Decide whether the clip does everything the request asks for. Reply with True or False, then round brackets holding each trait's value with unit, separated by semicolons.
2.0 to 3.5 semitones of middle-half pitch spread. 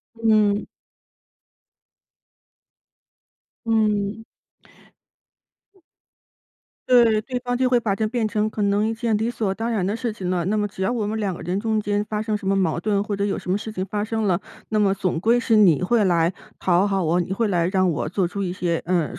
True (2.8 semitones)